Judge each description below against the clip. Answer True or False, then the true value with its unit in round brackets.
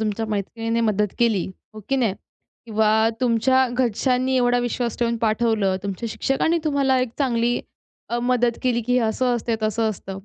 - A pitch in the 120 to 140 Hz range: False (235 Hz)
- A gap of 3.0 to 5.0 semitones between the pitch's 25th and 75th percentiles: False (2.5 semitones)